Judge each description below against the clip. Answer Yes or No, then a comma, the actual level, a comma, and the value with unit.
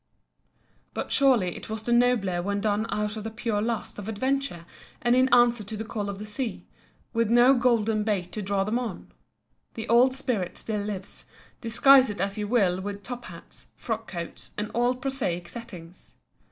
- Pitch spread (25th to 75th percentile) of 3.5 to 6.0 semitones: No, average, 3.1 semitones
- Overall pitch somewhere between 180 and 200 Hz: No, high, 220 Hz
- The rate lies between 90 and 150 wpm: No, average, 185 wpm